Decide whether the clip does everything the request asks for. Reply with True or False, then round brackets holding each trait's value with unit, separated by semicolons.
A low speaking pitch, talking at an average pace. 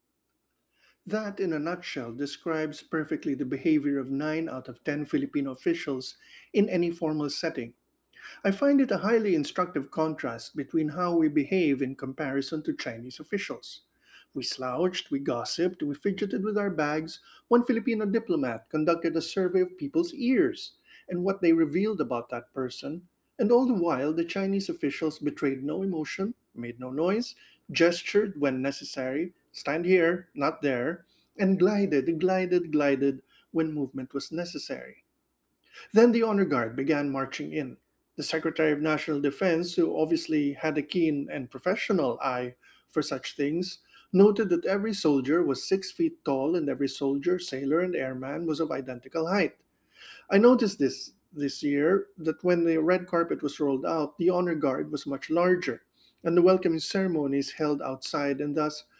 False (165 Hz; 160 wpm)